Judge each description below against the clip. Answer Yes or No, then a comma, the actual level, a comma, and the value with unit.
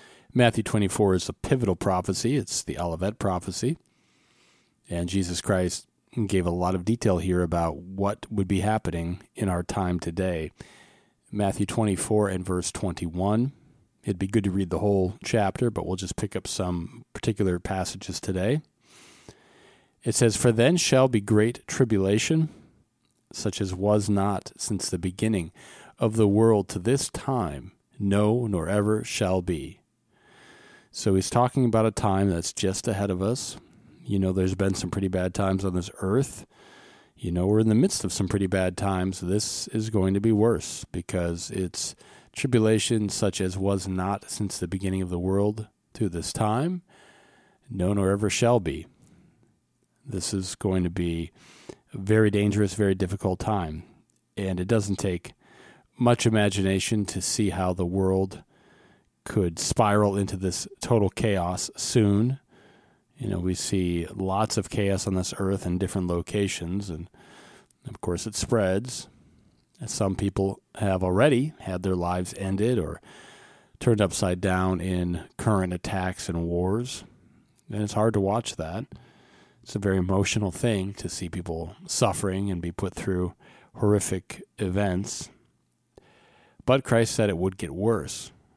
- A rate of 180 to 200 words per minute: No, average, 155 wpm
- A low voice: Yes, low, 100 Hz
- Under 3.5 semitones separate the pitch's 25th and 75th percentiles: Yes, average, 3.0 semitones